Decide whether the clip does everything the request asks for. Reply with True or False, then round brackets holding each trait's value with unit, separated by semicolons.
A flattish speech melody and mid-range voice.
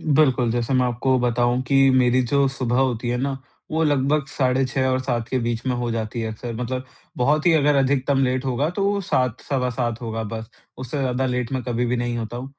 False (2.0 semitones; 125 Hz)